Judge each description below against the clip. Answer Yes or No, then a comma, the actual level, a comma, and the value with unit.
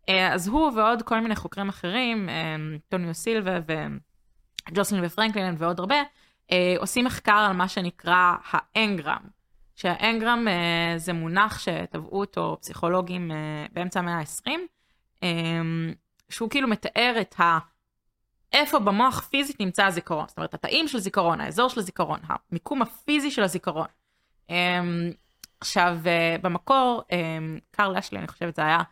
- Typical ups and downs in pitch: Yes, average, 4.5 semitones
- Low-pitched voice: No, medium, 185 Hz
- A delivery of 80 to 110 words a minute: No, average, 120 wpm